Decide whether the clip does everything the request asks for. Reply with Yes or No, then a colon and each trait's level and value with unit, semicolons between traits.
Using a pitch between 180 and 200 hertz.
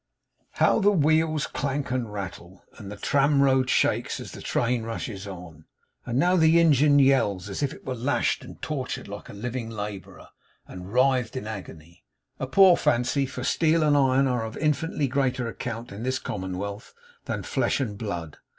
No: low, 125 Hz